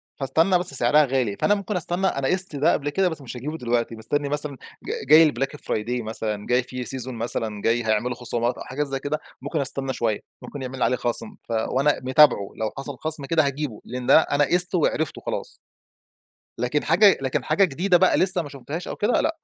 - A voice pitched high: No, low, 135 Hz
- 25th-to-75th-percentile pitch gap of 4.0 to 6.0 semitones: Yes, average, 4.4 semitones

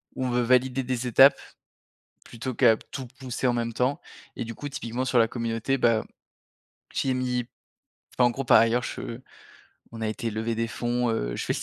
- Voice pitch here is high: No, low, 120 Hz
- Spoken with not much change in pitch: Yes, narrow, 1.8 semitones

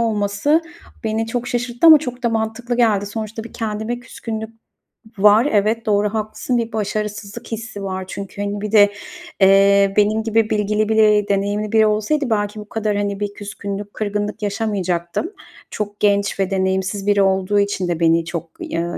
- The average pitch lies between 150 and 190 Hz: No, high, 210 Hz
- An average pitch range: No, narrow, 1.7 semitones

